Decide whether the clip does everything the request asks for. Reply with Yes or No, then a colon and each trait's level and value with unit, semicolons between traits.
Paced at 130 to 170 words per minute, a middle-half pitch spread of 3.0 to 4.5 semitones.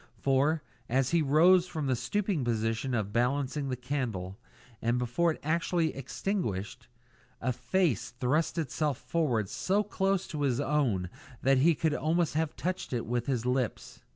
No: average, 160 wpm; average, 4.9 semitones